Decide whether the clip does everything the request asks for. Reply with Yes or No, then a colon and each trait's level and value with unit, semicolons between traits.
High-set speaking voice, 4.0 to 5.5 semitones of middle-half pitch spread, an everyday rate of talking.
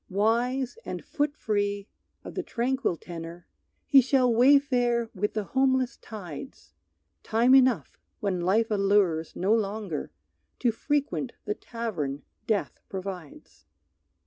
No: high, 220 Hz; average, 4.7 semitones; slow, 120 wpm